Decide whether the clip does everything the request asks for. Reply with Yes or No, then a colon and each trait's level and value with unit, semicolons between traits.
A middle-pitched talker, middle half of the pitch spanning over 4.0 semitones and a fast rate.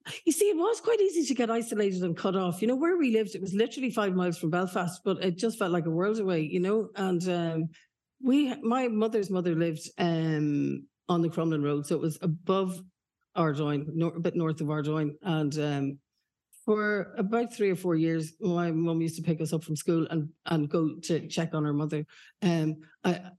Yes: medium, 175 Hz; average, 4.5 semitones; fast, 215 wpm